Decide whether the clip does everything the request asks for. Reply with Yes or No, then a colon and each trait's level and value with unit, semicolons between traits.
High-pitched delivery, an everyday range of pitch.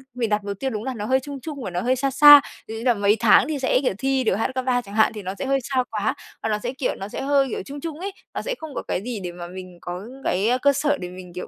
Yes: high, 245 Hz; average, 5.0 semitones